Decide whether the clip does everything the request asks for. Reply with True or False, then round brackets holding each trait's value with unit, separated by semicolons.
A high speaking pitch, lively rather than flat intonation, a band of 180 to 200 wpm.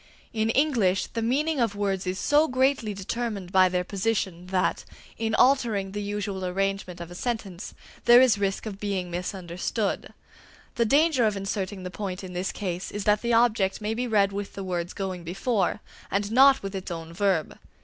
False (200 Hz; 3.5 semitones; 185 wpm)